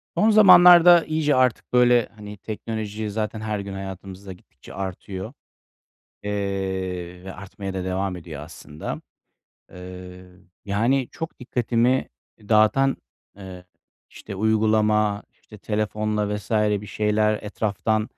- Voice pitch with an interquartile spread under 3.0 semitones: Yes, narrow, 2.6 semitones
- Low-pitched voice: Yes, low, 105 Hz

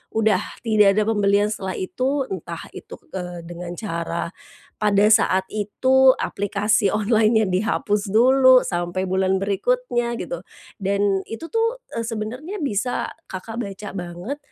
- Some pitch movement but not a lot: Yes, average, 3.8 semitones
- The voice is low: No, high, 210 Hz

